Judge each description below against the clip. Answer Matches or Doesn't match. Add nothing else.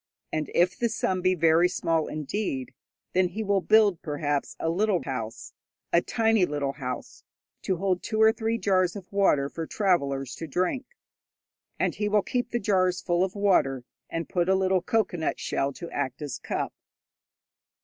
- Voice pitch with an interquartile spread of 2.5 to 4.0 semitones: Doesn't match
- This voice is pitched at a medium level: Matches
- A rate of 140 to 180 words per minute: Matches